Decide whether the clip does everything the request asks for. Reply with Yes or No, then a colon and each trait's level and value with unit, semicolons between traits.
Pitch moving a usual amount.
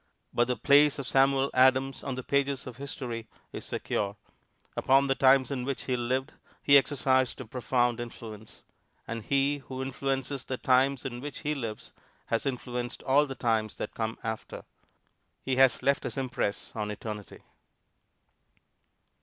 No: narrow, 2.3 semitones